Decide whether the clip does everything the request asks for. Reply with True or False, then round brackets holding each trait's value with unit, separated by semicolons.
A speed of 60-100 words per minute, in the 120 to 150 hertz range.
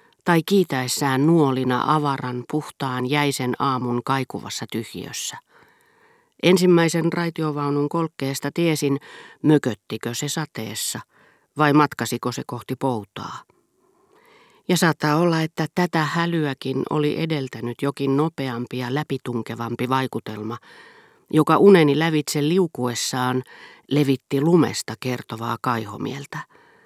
True (95 wpm; 140 Hz)